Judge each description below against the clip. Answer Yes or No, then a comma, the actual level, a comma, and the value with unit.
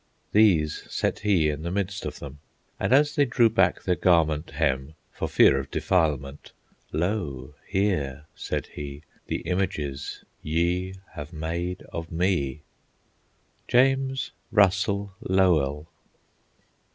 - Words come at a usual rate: No, slow, 120 wpm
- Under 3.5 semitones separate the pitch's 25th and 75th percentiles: No, average, 4.9 semitones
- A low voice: Yes, very low, 85 Hz